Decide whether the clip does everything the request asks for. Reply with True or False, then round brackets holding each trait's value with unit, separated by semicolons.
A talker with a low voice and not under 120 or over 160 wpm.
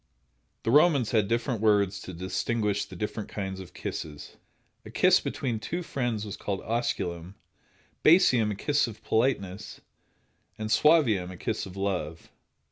True (105 Hz; 145 wpm)